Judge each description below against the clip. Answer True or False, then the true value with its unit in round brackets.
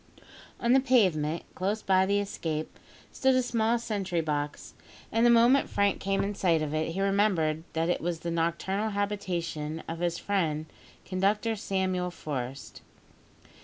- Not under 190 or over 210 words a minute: False (155 wpm)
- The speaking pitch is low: False (190 Hz)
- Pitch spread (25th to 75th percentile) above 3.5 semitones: True (4.2 semitones)